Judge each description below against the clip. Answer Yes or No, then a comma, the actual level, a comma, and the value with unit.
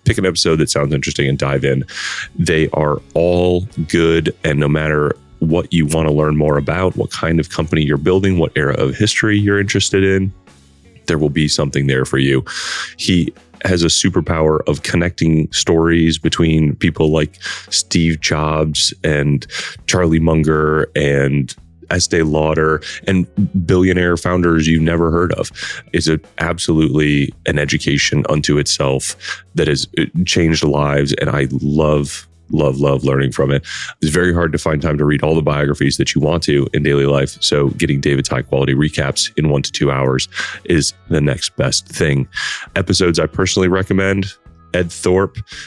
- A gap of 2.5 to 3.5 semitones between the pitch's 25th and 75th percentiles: Yes, average, 3.2 semitones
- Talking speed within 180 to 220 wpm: No, average, 165 wpm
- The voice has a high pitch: No, very low, 80 Hz